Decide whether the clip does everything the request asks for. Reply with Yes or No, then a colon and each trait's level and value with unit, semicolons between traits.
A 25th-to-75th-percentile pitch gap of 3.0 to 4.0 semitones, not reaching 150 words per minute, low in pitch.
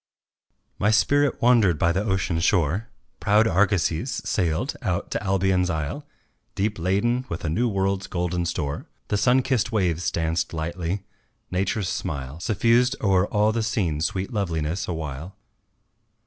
No: average, 4.4 semitones; average, 140 wpm; very low, 95 Hz